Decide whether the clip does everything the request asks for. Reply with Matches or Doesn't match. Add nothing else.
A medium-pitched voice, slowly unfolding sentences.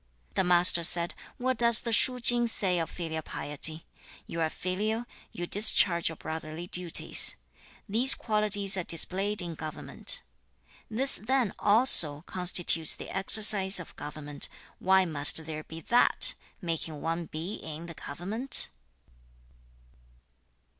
Matches